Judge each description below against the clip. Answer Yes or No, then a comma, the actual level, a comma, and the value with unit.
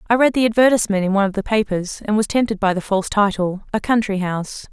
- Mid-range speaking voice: No, high, 205 Hz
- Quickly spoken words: Yes, fast, 240 wpm